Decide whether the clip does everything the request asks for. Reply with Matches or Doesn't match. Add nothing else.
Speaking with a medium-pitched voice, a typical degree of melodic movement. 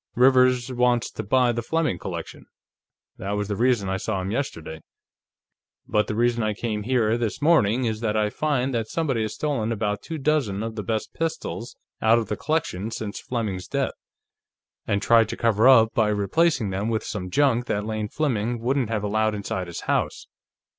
Doesn't match